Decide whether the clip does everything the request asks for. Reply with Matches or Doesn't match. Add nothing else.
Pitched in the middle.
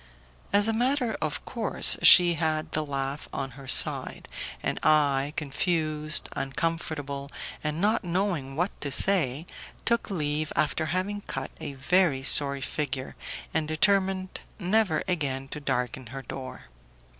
Matches